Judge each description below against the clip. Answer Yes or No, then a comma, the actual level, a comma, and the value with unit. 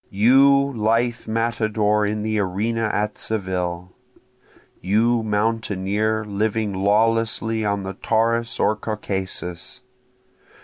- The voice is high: No, low, 110 Hz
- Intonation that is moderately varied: No, narrow, 2.0 semitones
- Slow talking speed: Yes, slow, 95 wpm